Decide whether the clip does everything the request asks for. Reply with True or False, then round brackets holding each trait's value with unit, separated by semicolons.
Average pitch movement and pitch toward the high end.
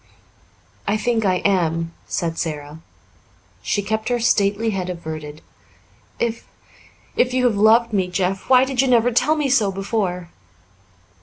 True (4.8 semitones; 205 Hz)